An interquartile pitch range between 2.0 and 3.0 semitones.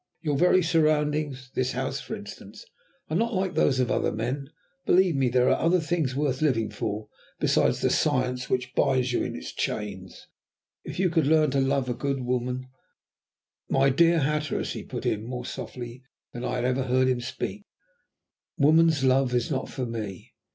No: average, 3.6 semitones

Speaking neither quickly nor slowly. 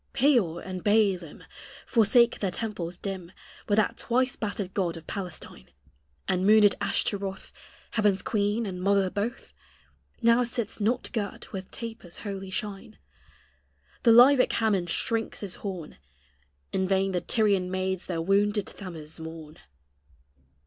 No: slow, 130 wpm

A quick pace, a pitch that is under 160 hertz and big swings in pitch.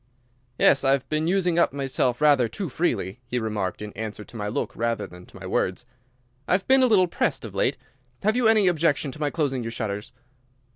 Yes: fast, 220 wpm; low, 135 Hz; wide, 7.7 semitones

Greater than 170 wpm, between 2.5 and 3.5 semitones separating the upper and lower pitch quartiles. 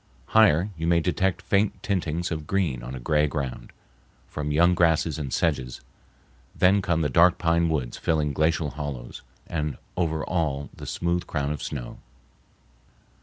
No: average, 155 wpm; average, 2.9 semitones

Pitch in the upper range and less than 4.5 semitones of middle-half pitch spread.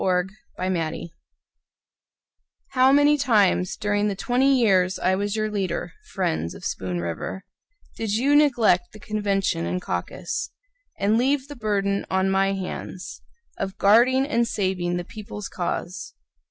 Yes: high, 200 Hz; average, 4.0 semitones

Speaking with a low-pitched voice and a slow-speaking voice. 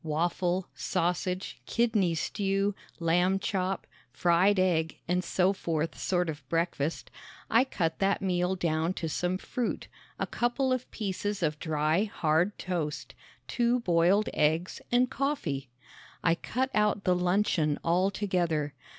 No: medium, 180 Hz; slow, 130 wpm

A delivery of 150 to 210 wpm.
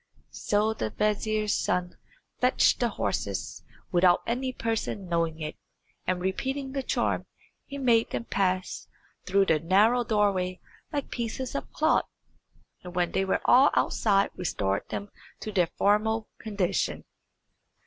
No: slow, 135 wpm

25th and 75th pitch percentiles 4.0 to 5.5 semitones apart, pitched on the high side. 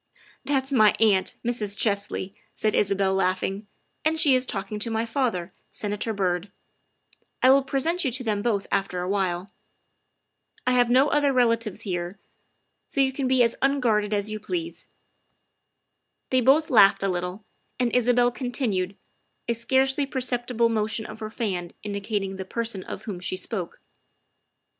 Yes: average, 4.4 semitones; high, 220 Hz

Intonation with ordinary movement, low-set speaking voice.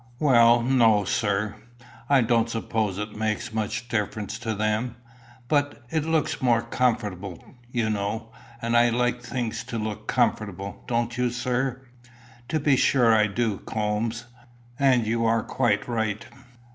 No: narrow, 2.3 semitones; low, 115 Hz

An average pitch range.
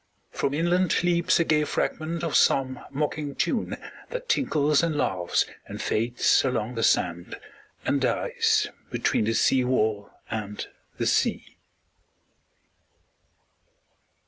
No: wide, 6.7 semitones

